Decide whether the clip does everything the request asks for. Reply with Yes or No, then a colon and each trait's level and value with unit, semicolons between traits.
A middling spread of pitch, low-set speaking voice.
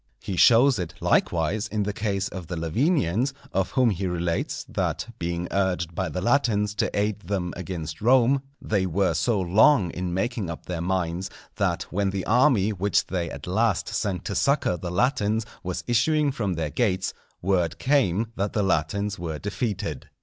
Yes: average, 4.0 semitones; very low, 95 Hz